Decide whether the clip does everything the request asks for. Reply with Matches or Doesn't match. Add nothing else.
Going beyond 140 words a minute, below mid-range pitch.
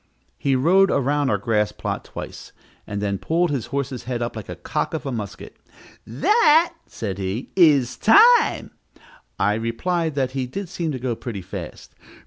Matches